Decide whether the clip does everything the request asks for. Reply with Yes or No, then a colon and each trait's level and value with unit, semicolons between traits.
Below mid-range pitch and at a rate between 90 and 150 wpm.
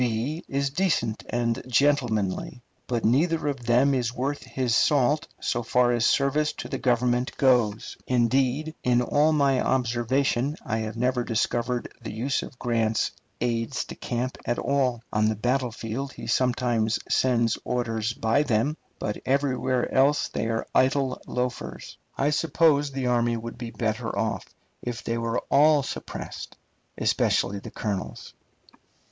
Yes: low, 125 Hz; average, 145 wpm